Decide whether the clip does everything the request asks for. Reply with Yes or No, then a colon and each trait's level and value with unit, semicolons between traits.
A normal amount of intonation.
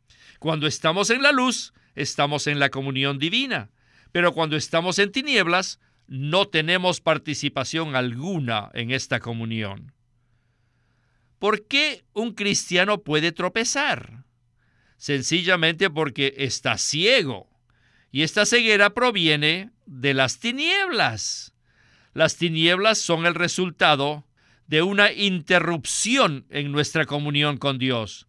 No: wide, 6.0 semitones